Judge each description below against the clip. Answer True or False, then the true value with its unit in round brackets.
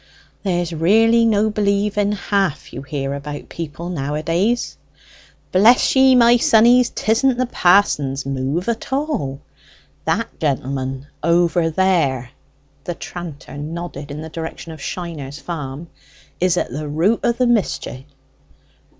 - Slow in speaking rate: True (125 wpm)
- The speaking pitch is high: False (170 Hz)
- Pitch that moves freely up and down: True (6.5 semitones)